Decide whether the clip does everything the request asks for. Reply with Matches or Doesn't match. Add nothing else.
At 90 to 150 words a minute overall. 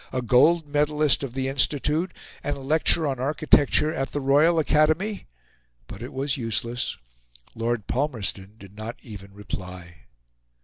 Matches